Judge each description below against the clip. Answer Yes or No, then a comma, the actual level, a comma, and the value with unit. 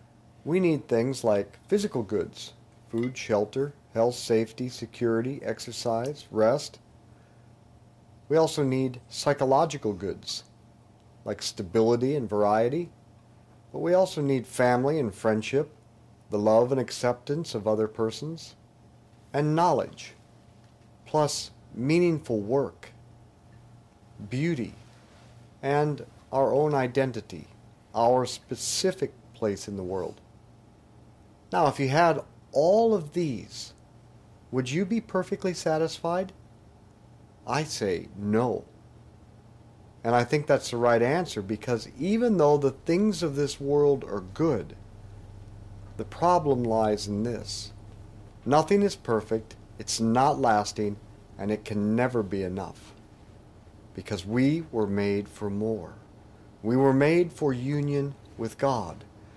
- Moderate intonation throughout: Yes, average, 4.4 semitones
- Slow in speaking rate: Yes, slow, 115 wpm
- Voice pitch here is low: Yes, low, 115 Hz